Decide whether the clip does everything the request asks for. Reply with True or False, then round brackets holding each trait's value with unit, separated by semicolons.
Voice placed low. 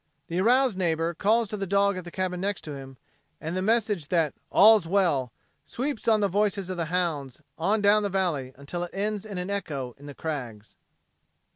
False (185 Hz)